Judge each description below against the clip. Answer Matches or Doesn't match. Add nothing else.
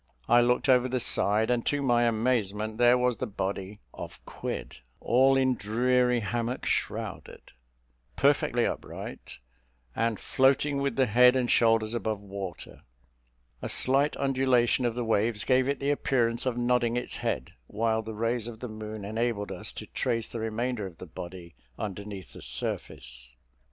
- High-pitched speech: Doesn't match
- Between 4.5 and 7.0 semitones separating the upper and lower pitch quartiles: Doesn't match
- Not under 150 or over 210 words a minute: Matches